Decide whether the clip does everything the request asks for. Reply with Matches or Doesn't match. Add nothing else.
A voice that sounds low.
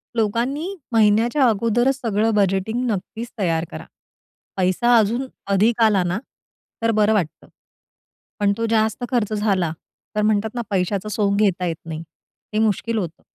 Doesn't match